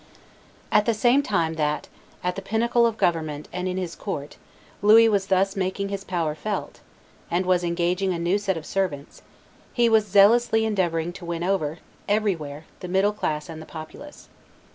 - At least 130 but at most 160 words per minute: No, average, 175 wpm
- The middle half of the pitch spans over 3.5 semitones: Yes, average, 3.9 semitones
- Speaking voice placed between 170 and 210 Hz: Yes, medium, 185 Hz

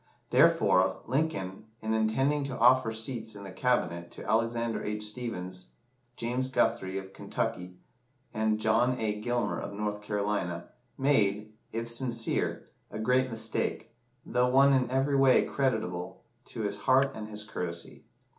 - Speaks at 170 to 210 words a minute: No, average, 140 wpm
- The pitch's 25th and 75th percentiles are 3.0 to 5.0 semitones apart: Yes, average, 3.5 semitones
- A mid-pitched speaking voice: No, low, 110 Hz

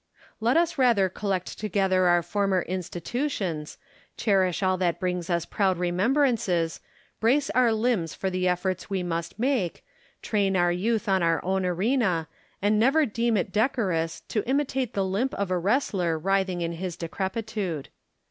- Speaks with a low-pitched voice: No, high, 190 Hz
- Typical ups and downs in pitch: Yes, average, 4.1 semitones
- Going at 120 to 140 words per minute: No, average, 155 wpm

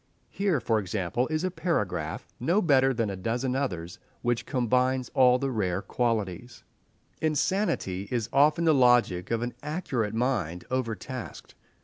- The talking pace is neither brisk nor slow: No, slow, 130 wpm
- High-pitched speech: No, low, 125 Hz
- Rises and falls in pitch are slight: No, average, 4.3 semitones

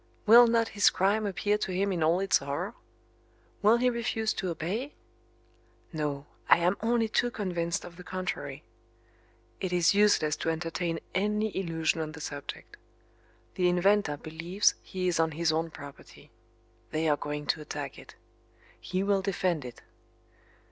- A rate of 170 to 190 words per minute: No, average, 155 wpm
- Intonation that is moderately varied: Yes, average, 4.3 semitones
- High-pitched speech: No, medium, 180 Hz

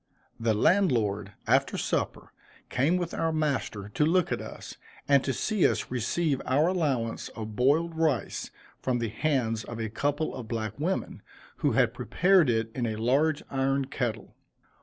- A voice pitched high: No, low, 135 Hz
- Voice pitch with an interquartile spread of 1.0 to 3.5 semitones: No, wide, 5.6 semitones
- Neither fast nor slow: Yes, average, 160 wpm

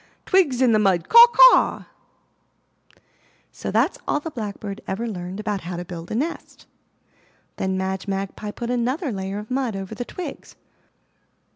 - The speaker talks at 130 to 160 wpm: Yes, average, 155 wpm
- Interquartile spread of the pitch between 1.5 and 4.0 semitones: No, average, 5.1 semitones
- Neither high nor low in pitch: No, high, 210 Hz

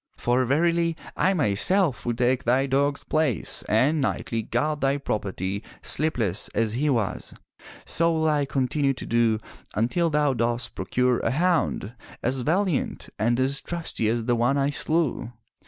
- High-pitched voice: No, low, 135 Hz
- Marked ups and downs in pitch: No, average, 4.5 semitones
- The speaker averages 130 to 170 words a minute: Yes, average, 155 wpm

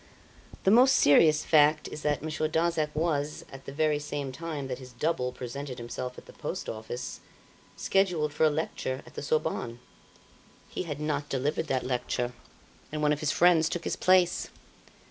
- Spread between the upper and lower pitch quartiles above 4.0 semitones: No, average, 3.1 semitones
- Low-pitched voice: No, medium, 150 Hz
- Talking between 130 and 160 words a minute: No, average, 175 wpm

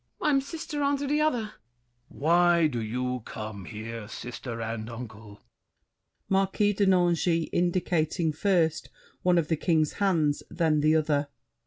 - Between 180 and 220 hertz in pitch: No, medium, 160 Hz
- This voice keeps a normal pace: Yes, average, 150 wpm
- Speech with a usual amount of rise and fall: No, wide, 7.5 semitones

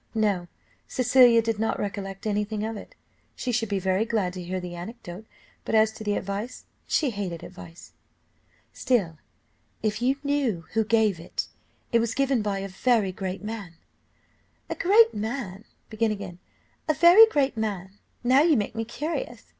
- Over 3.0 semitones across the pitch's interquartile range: Yes, average, 3.9 semitones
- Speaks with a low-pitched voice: No, high, 220 Hz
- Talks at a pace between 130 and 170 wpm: Yes, average, 155 wpm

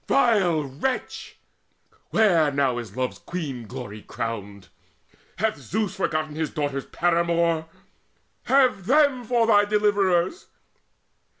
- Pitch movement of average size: No, wide, 7.5 semitones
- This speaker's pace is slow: Yes, slow, 105 wpm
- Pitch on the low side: No, medium, 170 Hz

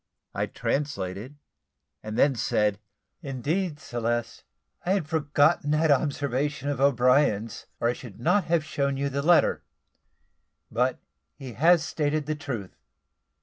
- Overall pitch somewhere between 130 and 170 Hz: Yes, medium, 140 Hz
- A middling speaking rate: No, slow, 130 wpm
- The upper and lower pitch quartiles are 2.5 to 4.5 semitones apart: Yes, average, 4.0 semitones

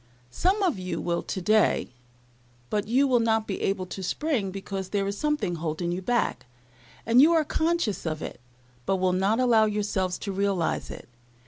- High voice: Yes, high, 200 Hz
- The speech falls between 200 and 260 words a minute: No, average, 180 wpm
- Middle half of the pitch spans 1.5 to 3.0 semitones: No, average, 4.7 semitones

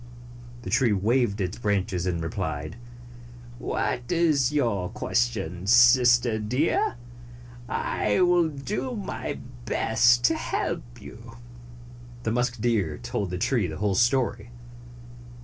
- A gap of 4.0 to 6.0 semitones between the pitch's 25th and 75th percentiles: Yes, average, 4.3 semitones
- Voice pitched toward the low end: Yes, low, 115 Hz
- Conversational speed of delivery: No, slow, 115 wpm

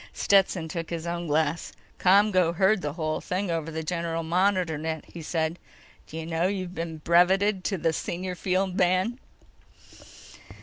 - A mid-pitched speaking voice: Yes, medium, 170 Hz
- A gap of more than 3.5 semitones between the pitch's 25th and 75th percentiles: No, narrow, 2.4 semitones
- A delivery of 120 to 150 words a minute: Yes, average, 145 wpm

